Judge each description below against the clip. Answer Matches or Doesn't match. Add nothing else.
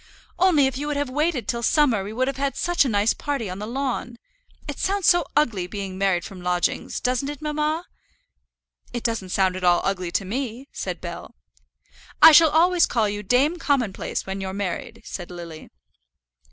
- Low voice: Doesn't match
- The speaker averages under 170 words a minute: Doesn't match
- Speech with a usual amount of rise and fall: Doesn't match